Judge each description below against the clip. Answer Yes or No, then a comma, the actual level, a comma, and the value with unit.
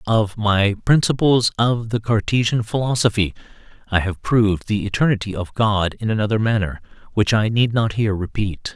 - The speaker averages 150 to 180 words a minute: Yes, average, 160 wpm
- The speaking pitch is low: Yes, low, 110 Hz